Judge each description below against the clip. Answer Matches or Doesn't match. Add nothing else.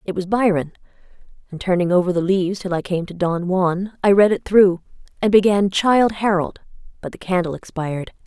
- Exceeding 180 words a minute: Matches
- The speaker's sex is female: Matches